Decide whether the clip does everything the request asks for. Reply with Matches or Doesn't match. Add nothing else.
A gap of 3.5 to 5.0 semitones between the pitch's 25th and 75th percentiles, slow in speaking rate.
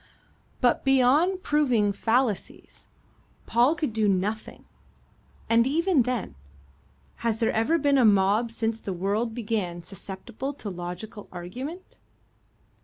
Matches